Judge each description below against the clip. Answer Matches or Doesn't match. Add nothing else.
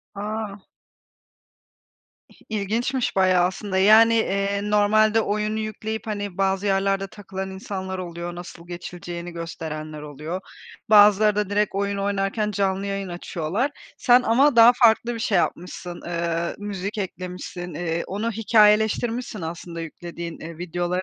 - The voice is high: Matches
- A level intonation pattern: Doesn't match